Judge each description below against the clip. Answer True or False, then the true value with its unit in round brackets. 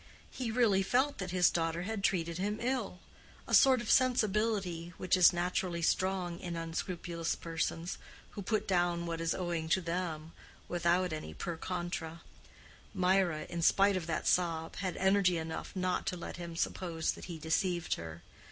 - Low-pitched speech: False (175 Hz)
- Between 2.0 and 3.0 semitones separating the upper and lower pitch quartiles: True (2.4 semitones)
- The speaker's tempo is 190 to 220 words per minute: False (160 wpm)